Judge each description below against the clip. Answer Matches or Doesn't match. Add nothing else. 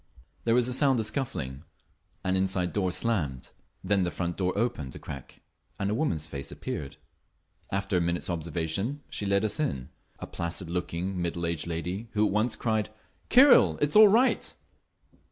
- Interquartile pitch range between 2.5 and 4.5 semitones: Doesn't match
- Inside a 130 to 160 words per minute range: Doesn't match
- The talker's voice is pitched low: Matches